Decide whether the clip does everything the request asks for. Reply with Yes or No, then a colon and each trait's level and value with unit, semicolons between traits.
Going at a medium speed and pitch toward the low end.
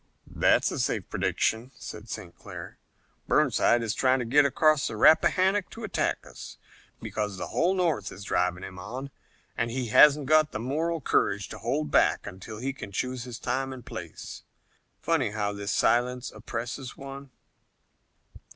Yes: average, 160 wpm; low, 125 Hz